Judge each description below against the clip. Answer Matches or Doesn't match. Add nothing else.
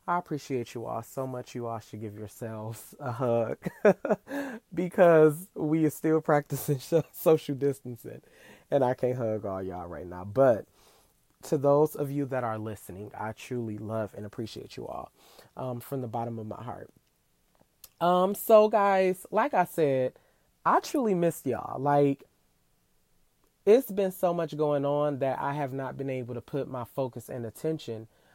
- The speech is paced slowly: Doesn't match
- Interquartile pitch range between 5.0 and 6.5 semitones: Matches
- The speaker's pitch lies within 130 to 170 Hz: Matches